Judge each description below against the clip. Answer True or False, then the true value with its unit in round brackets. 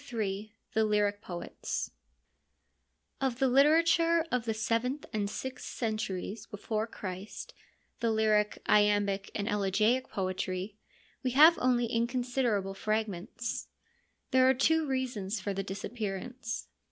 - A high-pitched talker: True (220 Hz)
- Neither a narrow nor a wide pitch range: True (3.9 semitones)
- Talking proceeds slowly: True (115 wpm)